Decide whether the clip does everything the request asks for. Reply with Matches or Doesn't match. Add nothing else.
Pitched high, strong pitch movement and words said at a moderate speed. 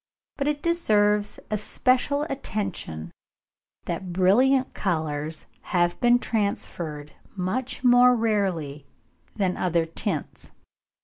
Doesn't match